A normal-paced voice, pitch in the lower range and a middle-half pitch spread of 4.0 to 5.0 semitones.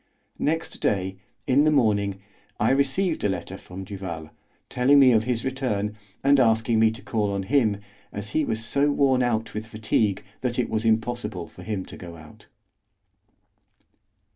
Yes: average, 165 wpm; low, 110 Hz; average, 4.5 semitones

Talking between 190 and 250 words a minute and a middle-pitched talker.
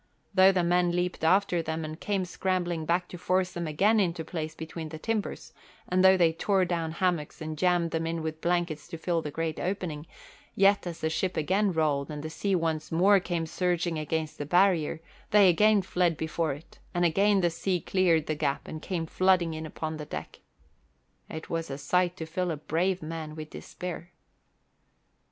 Yes: average, 195 wpm; medium, 170 Hz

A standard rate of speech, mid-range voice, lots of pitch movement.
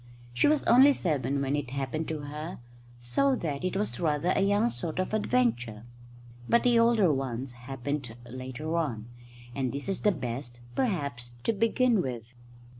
Yes: average, 165 wpm; medium, 150 Hz; wide, 8.0 semitones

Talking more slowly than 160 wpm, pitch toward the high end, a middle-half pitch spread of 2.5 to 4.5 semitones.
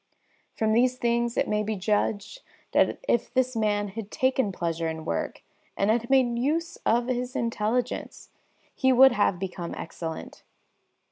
Yes: average, 150 wpm; high, 230 Hz; average, 3.7 semitones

